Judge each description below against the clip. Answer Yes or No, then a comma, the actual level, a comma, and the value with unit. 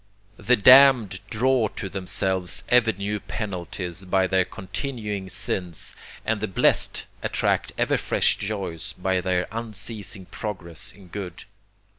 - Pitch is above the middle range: No, low, 100 Hz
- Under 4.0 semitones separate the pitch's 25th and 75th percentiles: Yes, average, 2.8 semitones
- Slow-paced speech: Yes, slow, 125 wpm